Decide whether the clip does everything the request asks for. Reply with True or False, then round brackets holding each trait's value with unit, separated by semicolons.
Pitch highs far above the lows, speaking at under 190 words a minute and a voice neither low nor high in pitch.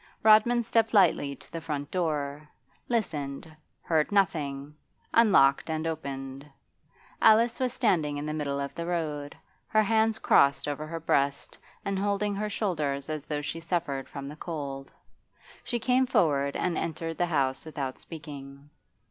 True (5.9 semitones; 150 wpm; 155 Hz)